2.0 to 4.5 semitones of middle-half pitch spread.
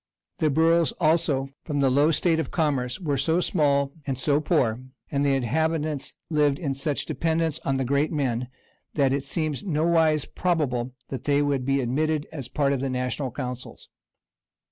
Yes: average, 2.8 semitones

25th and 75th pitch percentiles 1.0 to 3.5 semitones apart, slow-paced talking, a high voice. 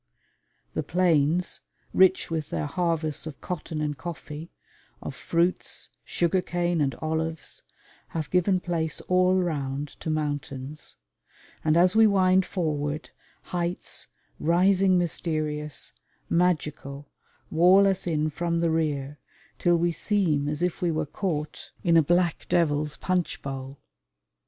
No: average, 3.0 semitones; slow, 125 wpm; medium, 165 Hz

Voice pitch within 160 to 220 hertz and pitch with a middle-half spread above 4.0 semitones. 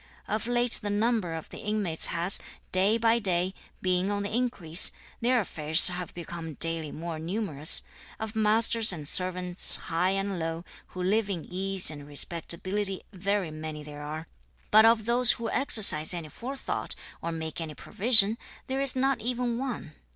Yes: high, 190 Hz; average, 5.1 semitones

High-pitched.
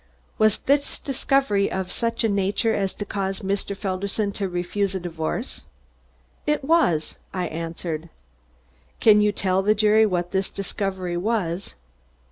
Yes: high, 195 Hz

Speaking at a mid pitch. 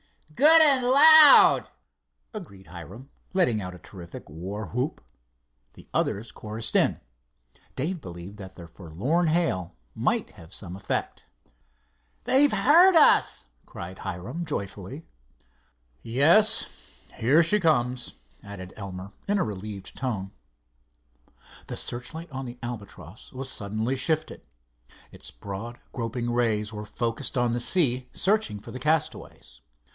No: low, 120 Hz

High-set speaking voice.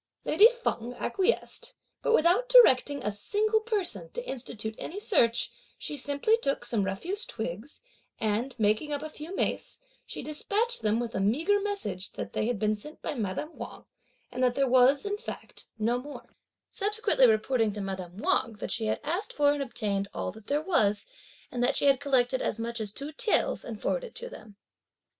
Yes: very high, 265 Hz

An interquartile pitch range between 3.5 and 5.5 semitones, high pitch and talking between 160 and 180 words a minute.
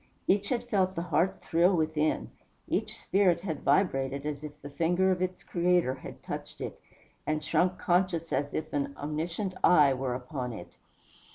No: average, 4.2 semitones; medium, 165 Hz; average, 170 wpm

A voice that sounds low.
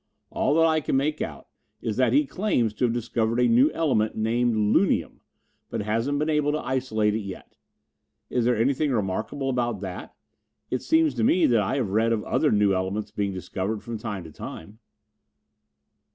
Yes: low, 115 Hz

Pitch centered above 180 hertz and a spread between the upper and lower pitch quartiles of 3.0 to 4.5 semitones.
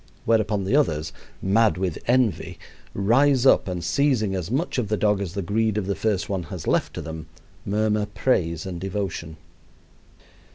No: low, 100 Hz; average, 3.4 semitones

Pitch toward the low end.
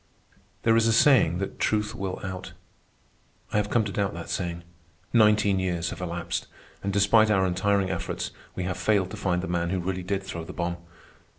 Yes: very low, 95 Hz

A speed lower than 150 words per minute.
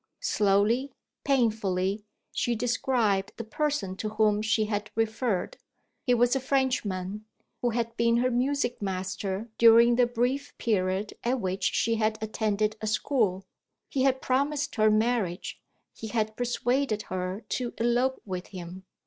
Yes: average, 140 wpm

